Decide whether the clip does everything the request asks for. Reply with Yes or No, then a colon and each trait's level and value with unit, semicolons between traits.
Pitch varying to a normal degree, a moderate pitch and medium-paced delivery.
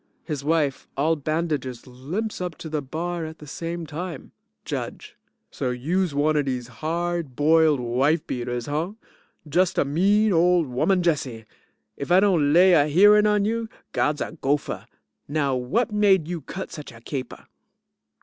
Yes: average, 4.1 semitones; medium, 155 Hz; average, 160 wpm